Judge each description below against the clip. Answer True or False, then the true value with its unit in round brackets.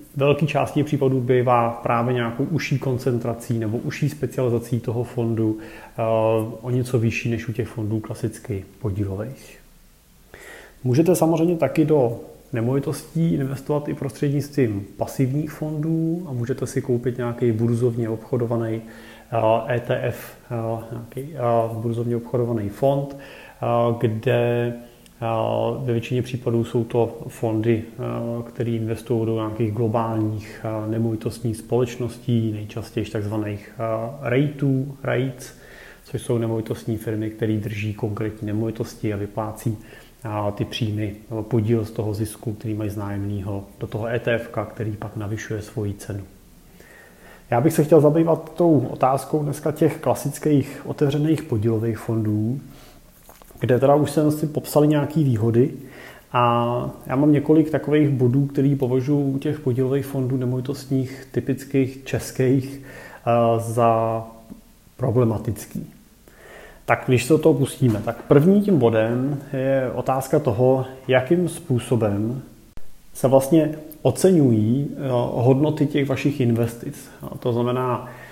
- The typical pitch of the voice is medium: False (120 Hz)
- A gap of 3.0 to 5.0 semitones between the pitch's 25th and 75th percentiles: True (3.3 semitones)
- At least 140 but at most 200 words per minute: False (115 wpm)